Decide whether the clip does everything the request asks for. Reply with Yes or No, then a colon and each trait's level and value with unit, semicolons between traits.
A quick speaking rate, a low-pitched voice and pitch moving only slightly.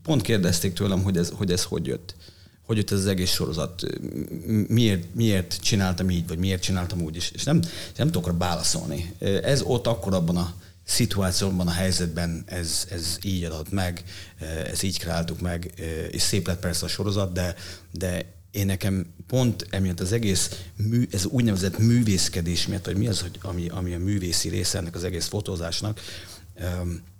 Yes: fast, 175 wpm; very low, 90 Hz; narrow, 2.2 semitones